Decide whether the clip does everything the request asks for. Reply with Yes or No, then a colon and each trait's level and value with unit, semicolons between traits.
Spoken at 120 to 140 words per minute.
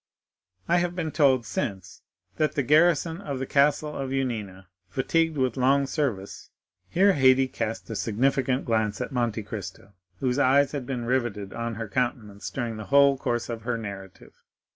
No: average, 165 wpm